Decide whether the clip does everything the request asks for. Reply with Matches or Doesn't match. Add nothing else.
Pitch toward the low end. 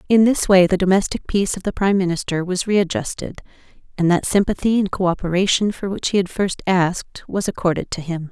Doesn't match